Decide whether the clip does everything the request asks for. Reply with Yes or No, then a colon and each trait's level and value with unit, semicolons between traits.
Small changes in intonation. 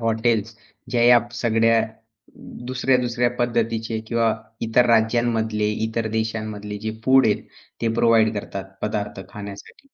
Yes: narrow, 1.4 semitones